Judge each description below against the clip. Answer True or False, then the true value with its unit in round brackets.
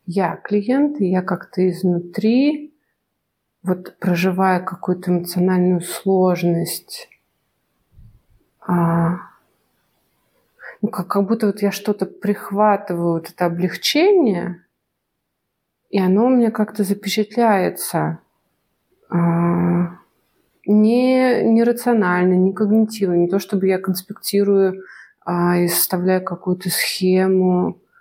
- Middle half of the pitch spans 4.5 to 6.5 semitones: False (2.9 semitones)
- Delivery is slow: True (95 wpm)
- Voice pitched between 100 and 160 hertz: False (185 Hz)